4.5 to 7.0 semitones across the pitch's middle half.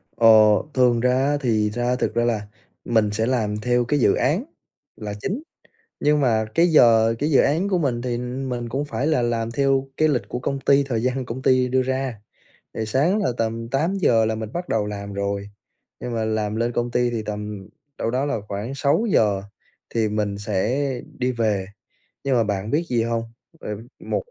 No: average, 3.6 semitones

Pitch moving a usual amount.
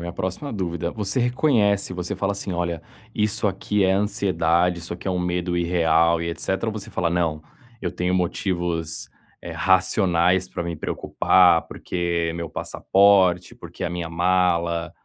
No: narrow, 2.1 semitones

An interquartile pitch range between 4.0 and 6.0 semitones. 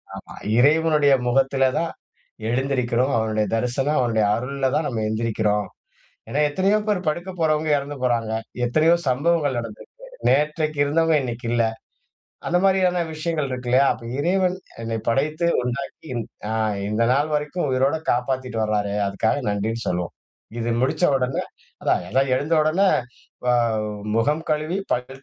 Yes: average, 4.8 semitones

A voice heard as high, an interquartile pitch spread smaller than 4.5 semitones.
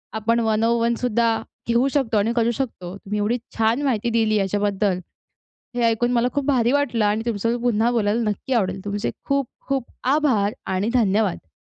Yes: high, 230 Hz; average, 2.7 semitones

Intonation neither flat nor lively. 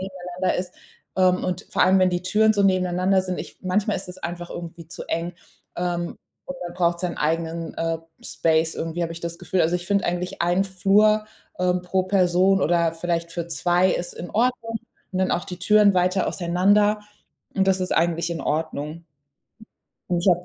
No: narrow, 1.7 semitones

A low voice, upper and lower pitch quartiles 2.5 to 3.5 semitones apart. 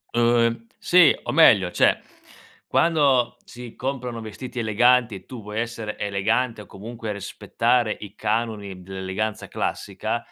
Yes: low, 115 Hz; average, 2.8 semitones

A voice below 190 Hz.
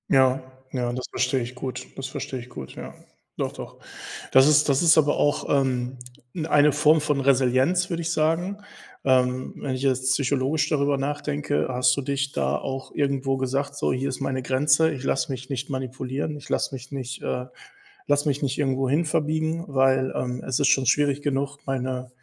Yes: low, 135 Hz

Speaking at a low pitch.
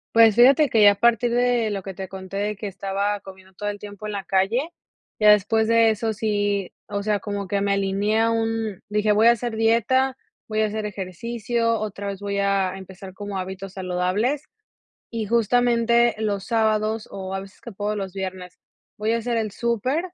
No: high, 210 Hz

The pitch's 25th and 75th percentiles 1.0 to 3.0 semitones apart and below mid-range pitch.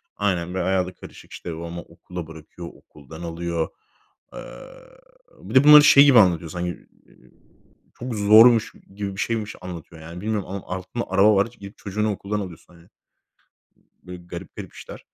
No: average, 3.5 semitones; very low, 95 Hz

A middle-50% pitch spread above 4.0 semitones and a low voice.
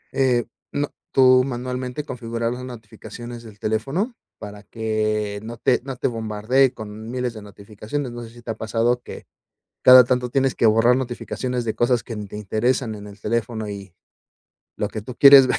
No: average, 2.8 semitones; low, 120 Hz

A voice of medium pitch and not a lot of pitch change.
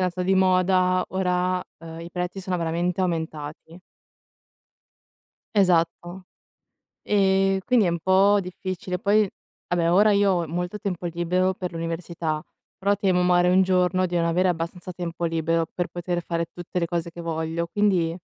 Yes: medium, 180 Hz; narrow, 1.9 semitones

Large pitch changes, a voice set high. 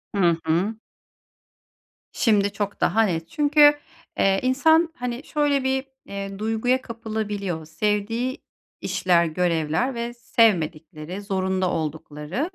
Yes: wide, 6.0 semitones; high, 205 Hz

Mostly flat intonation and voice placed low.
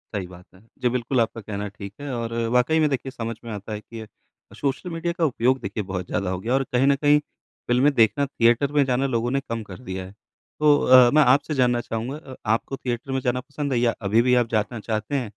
No: average, 3.6 semitones; low, 125 Hz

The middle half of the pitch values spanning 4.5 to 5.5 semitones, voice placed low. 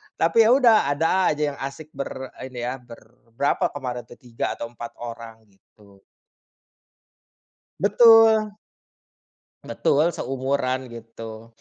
Yes: average, 5.2 semitones; low, 130 Hz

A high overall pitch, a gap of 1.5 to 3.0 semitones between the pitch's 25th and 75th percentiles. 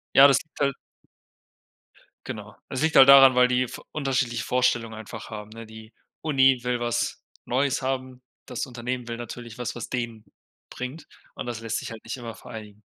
No: low, 125 Hz; narrow, 2.4 semitones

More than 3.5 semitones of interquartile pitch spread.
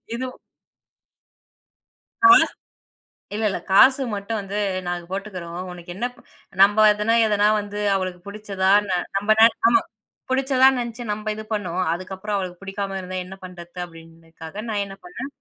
No: average, 3.0 semitones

